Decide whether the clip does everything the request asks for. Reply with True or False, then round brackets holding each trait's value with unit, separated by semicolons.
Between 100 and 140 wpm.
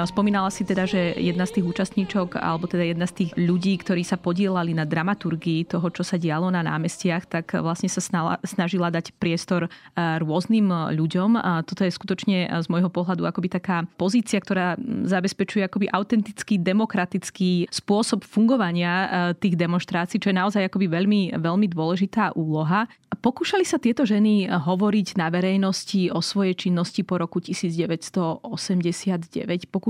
False (150 wpm)